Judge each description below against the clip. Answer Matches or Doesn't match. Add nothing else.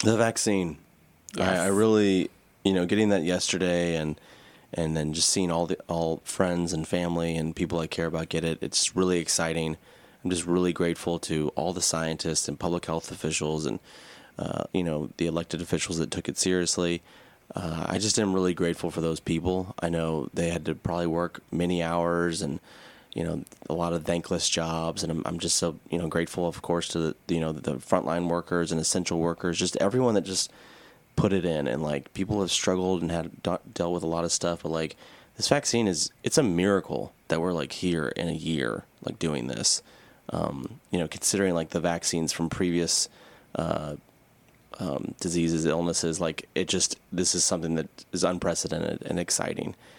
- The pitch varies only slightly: Matches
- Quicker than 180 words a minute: Matches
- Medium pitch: Doesn't match